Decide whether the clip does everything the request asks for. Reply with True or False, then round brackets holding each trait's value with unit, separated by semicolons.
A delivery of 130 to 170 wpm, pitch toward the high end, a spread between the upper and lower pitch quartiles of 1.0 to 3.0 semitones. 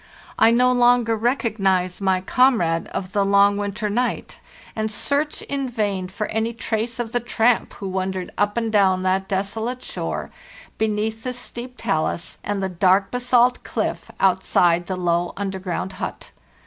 False (160 wpm; 205 Hz; 3.9 semitones)